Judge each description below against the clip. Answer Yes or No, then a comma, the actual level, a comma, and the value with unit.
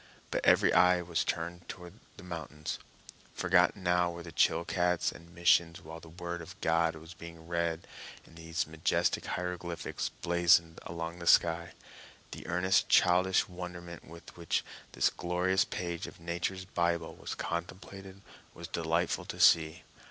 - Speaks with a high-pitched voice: No, very low, 85 Hz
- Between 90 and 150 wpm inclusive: Yes, average, 145 wpm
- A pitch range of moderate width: No, narrow, 1.2 semitones